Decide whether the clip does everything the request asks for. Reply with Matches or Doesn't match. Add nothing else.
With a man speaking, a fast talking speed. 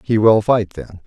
Matches